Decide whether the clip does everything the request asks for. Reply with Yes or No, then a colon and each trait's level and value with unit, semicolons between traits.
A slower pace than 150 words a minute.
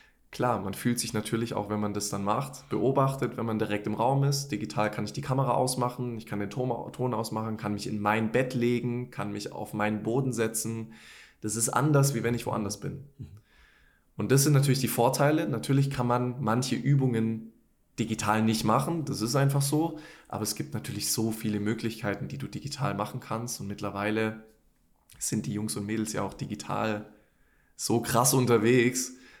No: fast, 190 wpm